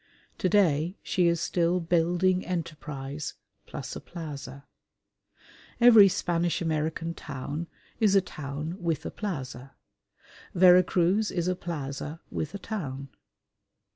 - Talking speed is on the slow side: Yes, slow, 120 wpm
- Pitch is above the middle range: No, medium, 170 Hz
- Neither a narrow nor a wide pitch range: Yes, average, 3.6 semitones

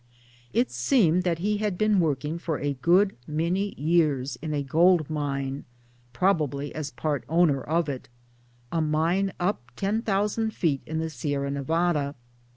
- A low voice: No, medium, 160 Hz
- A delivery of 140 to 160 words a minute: Yes, average, 150 wpm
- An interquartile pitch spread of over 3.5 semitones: Yes, average, 4.1 semitones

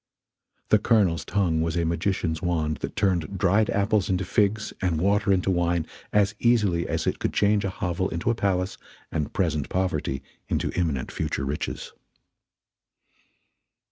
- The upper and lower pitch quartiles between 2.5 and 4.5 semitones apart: Yes, average, 3.4 semitones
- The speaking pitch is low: Yes, very low, 90 Hz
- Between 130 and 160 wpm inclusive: Yes, average, 150 wpm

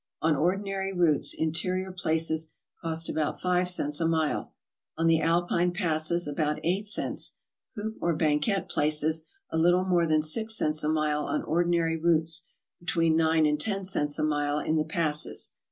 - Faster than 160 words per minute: Yes, average, 170 wpm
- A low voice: No, medium, 165 Hz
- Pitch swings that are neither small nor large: No, narrow, 2.3 semitones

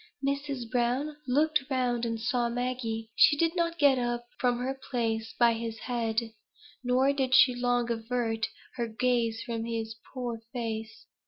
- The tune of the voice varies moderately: No, narrow, 2.2 semitones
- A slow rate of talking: No, average, 155 wpm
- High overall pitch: Yes, high, 245 Hz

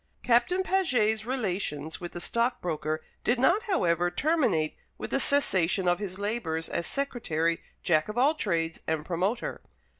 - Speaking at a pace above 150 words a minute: No, average, 145 wpm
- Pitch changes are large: Yes, wide, 7.1 semitones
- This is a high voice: Yes, high, 200 Hz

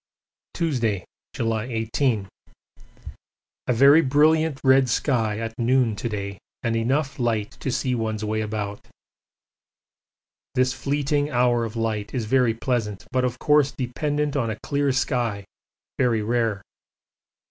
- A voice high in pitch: No, low, 120 Hz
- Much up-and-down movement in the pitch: No, average, 3.4 semitones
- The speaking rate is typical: No, slow, 130 wpm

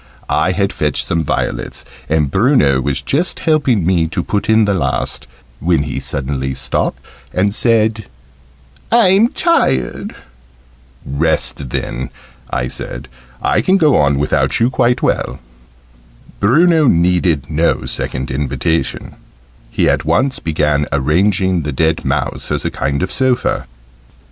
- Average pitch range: No, wide, 8.2 semitones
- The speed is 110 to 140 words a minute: Yes, slow, 135 wpm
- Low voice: Yes, very low, 85 Hz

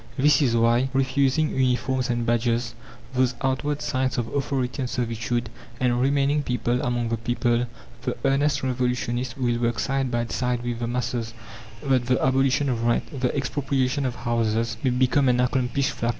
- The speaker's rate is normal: Yes, average, 165 wpm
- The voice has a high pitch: No, low, 125 Hz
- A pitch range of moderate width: No, narrow, 1.9 semitones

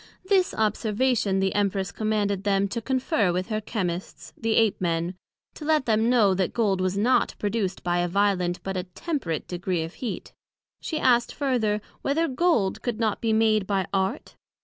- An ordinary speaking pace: Yes, average, 175 wpm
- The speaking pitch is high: Yes, high, 205 Hz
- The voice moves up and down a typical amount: Yes, average, 3.8 semitones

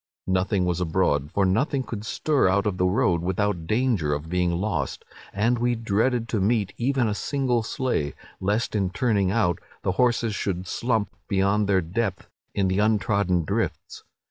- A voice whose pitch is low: Yes, low, 100 Hz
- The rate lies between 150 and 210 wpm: Yes, average, 170 wpm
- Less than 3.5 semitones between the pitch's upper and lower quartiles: No, average, 4.0 semitones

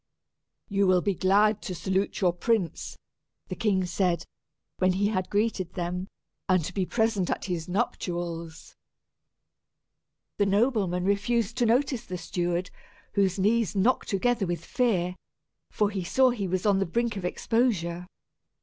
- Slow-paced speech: No, average, 150 wpm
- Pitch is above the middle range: Yes, high, 195 Hz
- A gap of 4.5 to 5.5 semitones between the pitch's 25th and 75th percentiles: No, average, 3.5 semitones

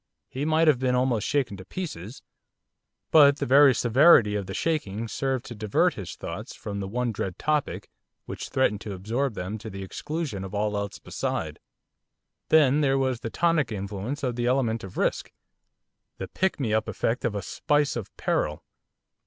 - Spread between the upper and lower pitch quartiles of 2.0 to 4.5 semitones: No, average, 5.3 semitones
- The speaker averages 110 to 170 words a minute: No, average, 180 wpm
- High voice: No, low, 120 Hz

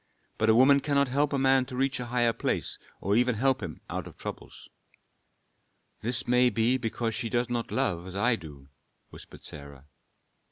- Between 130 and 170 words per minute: No, average, 185 wpm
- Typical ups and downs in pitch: Yes, average, 3.3 semitones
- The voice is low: Yes, low, 120 Hz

